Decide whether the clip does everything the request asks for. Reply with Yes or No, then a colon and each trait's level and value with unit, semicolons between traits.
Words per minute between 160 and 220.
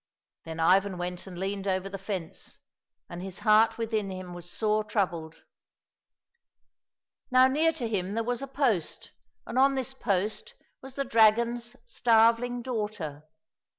No: average, 145 wpm